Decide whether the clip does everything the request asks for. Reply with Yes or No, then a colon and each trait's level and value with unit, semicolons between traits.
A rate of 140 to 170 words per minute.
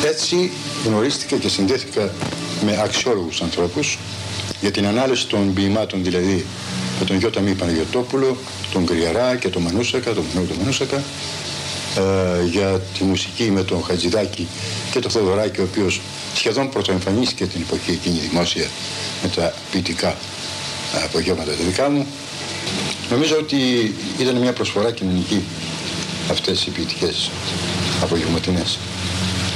No: average, 125 wpm